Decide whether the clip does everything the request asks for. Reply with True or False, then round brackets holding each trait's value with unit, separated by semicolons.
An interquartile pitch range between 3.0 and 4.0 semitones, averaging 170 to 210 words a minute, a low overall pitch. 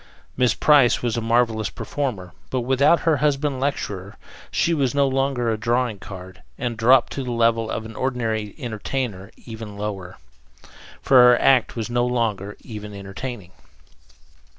False (3.7 semitones; 150 wpm; 120 Hz)